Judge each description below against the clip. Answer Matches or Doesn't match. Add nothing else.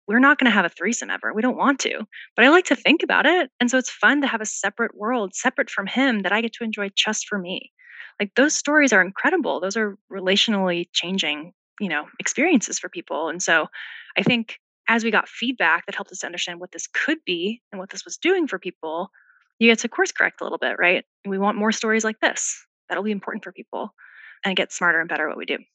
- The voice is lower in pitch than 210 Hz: Doesn't match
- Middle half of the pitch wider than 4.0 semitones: Matches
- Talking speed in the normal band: Doesn't match